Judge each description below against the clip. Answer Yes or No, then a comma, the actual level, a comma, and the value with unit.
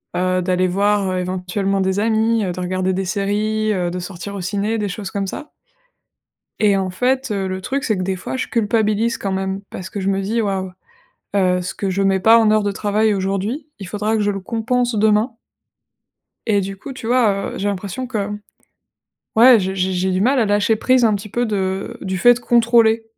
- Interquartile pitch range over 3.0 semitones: No, average, 2.7 semitones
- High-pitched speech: Yes, high, 200 Hz